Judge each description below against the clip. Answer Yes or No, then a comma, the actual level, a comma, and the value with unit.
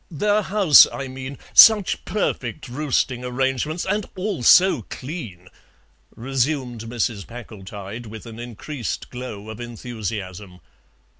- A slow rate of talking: Yes, slow, 115 wpm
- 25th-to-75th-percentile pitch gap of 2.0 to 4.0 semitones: No, average, 5.1 semitones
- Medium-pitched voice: No, low, 125 Hz